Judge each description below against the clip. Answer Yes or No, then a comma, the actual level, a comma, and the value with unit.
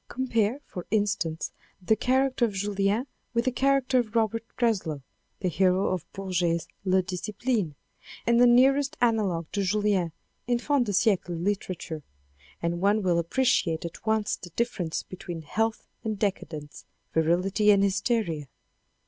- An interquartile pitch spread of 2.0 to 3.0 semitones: No, average, 4.8 semitones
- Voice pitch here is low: No, high, 200 Hz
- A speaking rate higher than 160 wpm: No, average, 145 wpm